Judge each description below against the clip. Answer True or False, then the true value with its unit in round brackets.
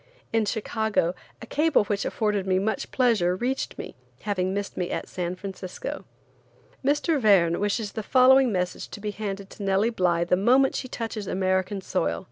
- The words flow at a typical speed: True (175 wpm)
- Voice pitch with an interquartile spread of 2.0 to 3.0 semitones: False (3.6 semitones)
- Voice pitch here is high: True (205 Hz)